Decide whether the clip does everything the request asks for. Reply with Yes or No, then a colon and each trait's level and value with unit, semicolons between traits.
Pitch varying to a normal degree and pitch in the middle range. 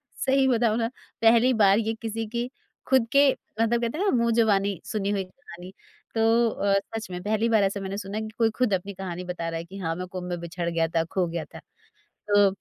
No: average, 4.0 semitones; high, 200 Hz